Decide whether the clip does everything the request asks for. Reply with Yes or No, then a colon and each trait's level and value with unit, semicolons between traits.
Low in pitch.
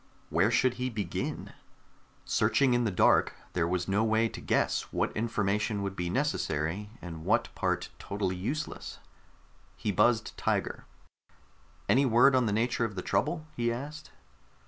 Yes: low, 110 Hz